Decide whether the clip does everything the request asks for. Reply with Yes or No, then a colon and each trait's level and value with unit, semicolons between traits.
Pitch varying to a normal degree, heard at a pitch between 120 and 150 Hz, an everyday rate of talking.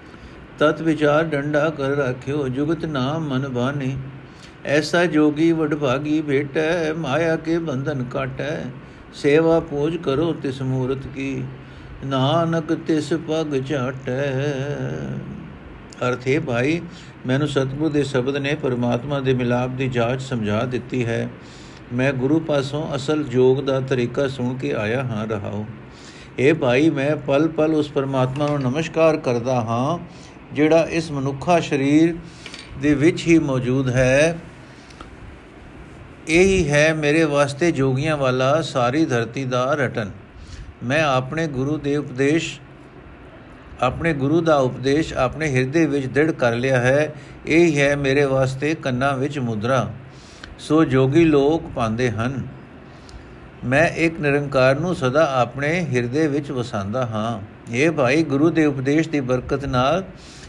Yes: average, 3.4 semitones; medium, 140 Hz; average, 130 wpm